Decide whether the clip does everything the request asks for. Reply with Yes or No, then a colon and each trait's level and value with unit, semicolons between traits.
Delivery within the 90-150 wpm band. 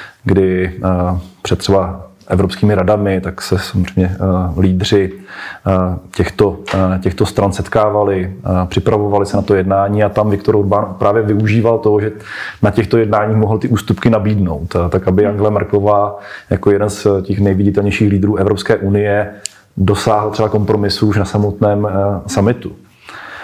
Yes: average, 135 wpm